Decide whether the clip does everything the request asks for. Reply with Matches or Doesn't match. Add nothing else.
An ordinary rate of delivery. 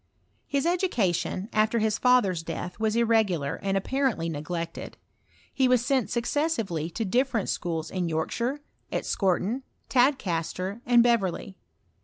Doesn't match